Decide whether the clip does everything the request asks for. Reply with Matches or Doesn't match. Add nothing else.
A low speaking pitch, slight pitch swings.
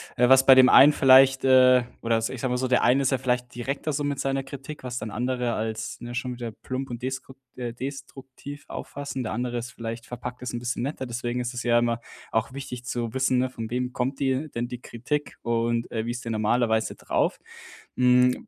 Matches